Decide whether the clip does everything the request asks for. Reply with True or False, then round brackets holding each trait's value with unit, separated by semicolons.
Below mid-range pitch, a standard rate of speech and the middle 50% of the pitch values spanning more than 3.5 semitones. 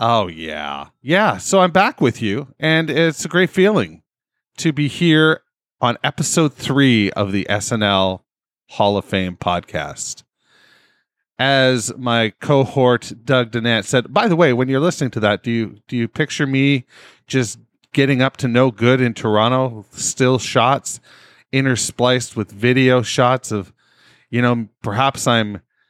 True (125 Hz; 150 wpm; 4.2 semitones)